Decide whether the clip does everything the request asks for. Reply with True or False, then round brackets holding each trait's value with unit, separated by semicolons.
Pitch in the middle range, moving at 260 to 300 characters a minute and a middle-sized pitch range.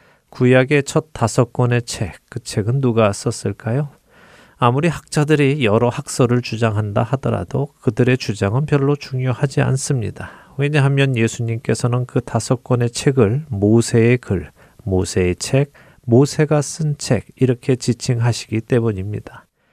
False (125 Hz; 295 characters per minute; 3.2 semitones)